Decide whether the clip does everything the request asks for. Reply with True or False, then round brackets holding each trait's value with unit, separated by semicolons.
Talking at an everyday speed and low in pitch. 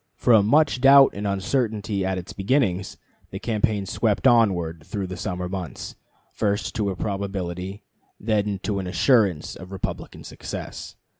True (145 wpm; 100 Hz)